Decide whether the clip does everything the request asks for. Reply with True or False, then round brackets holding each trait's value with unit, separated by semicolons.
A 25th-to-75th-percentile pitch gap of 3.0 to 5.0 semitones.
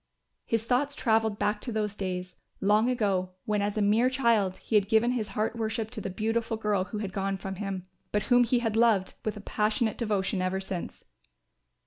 False (2.6 semitones)